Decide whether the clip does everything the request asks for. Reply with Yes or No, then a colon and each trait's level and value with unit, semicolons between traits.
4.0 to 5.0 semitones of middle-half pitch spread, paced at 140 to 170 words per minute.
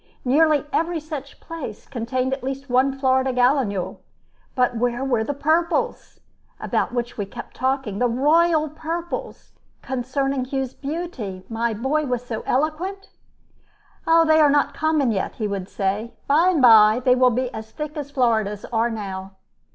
Yes: average, 4.5 semitones; average, 155 wpm